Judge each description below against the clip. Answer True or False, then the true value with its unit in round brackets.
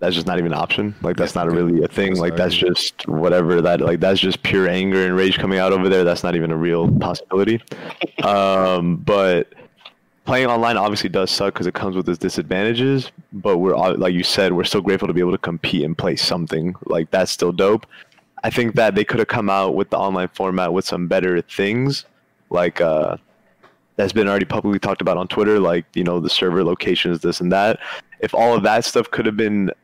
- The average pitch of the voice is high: False (95 Hz)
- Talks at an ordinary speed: False (225 wpm)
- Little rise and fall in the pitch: True (2.2 semitones)